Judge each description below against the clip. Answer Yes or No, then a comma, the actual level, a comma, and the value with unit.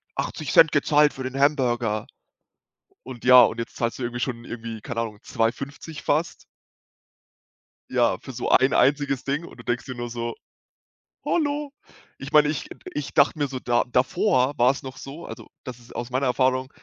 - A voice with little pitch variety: No, average, 3.0 semitones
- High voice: No, low, 130 Hz